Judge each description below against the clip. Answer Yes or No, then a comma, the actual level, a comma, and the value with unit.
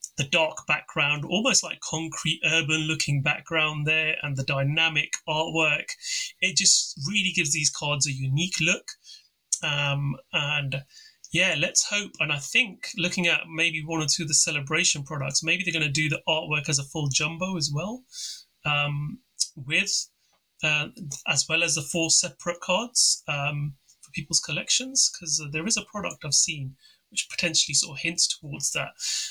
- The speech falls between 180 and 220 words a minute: No, average, 170 wpm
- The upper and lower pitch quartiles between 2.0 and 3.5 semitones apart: Yes, average, 2.9 semitones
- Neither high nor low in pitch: Yes, medium, 160 Hz